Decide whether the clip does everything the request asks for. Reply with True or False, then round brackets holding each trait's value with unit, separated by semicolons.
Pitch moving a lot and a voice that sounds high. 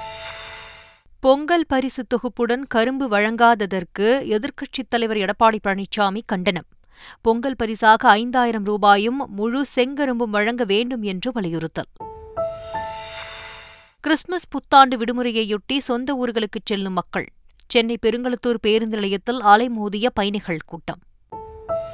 False (3.9 semitones; 230 Hz)